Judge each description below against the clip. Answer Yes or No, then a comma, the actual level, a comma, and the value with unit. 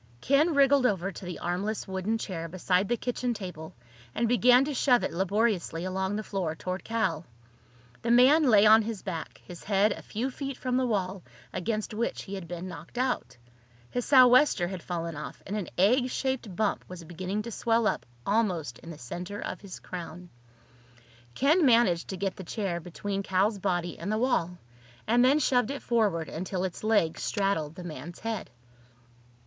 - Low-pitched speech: No, high, 200 Hz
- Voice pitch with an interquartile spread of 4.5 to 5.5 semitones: Yes, average, 4.9 semitones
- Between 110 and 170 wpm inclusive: No, average, 185 wpm